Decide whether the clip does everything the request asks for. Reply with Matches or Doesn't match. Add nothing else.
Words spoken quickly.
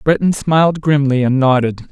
Doesn't match